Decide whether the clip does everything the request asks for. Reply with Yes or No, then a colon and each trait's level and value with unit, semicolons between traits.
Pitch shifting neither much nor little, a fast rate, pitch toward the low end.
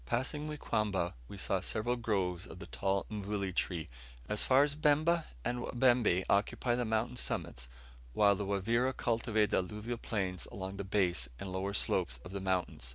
No: average, 4.3 semitones; average, 170 wpm; low, 105 Hz